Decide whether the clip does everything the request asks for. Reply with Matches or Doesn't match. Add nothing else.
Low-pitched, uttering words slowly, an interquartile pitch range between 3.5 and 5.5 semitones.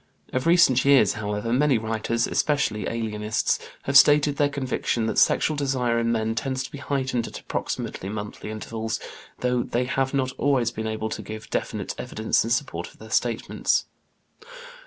Doesn't match